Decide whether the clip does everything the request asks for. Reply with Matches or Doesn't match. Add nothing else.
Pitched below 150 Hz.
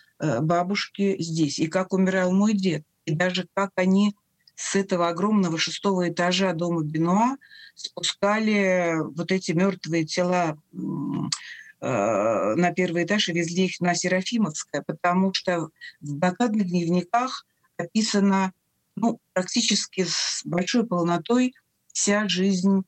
Doesn't match